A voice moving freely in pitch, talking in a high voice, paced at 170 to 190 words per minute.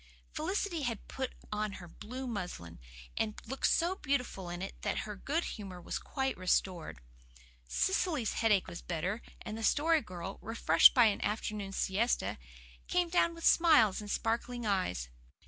No: wide, 6.0 semitones; high, 220 Hz; average, 155 wpm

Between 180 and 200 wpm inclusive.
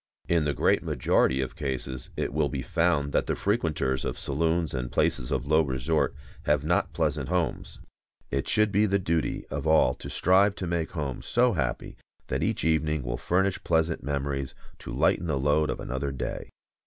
Yes: average, 185 wpm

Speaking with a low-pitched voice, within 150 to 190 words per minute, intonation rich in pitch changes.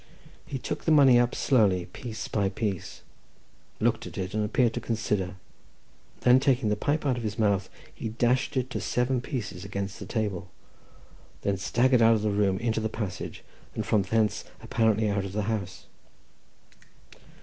No: low, 110 Hz; average, 170 wpm; average, 3.5 semitones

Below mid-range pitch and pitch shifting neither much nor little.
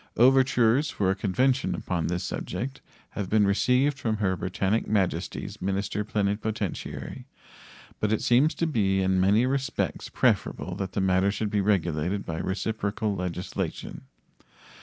Yes: low, 100 Hz; average, 3.3 semitones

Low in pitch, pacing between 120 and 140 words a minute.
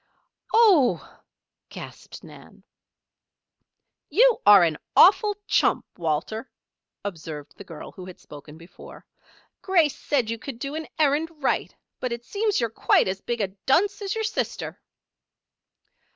No: high, 245 Hz; slow, 135 wpm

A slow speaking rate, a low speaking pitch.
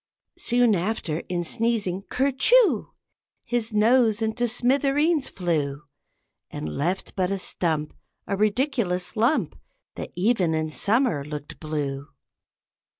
No: slow, 115 wpm; high, 205 Hz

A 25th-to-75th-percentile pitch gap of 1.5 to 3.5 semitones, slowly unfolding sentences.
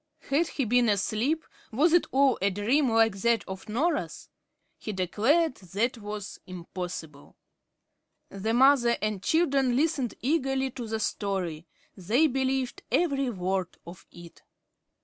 No: wide, 5.6 semitones; slow, 130 wpm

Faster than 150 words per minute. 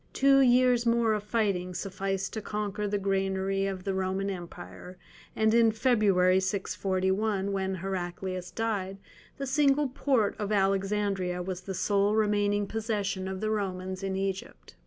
No: average, 145 wpm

